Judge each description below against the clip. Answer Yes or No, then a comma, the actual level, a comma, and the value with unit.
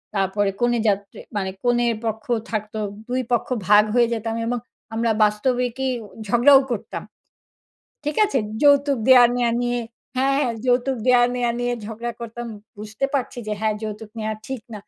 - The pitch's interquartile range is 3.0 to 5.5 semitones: No, narrow, 2.5 semitones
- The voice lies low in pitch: No, high, 240 Hz